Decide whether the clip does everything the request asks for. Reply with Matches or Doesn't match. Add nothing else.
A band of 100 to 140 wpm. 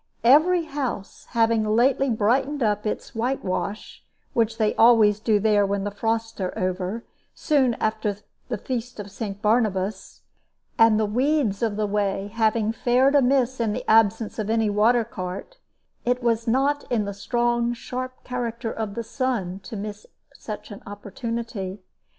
Doesn't match